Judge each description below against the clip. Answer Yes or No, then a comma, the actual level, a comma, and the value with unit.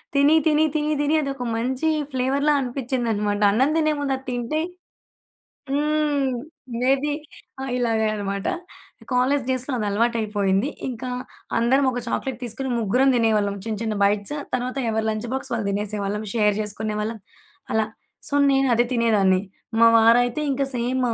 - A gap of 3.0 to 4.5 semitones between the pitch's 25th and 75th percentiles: Yes, average, 3.9 semitones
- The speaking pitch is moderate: No, high, 240 Hz